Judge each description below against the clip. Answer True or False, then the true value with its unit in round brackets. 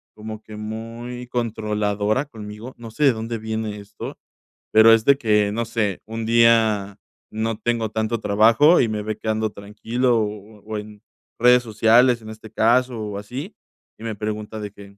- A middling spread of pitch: False (1.7 semitones)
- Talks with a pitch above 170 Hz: False (110 Hz)